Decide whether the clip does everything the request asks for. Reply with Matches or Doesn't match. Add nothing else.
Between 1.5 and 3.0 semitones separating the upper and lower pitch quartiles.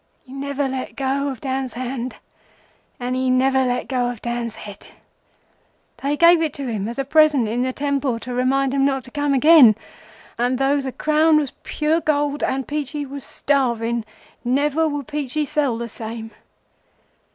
Matches